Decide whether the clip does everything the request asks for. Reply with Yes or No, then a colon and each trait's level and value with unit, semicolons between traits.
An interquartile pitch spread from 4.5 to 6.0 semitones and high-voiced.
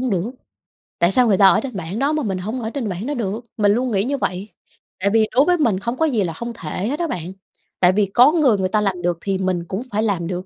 Yes: average, 4.9 semitones; high, 210 Hz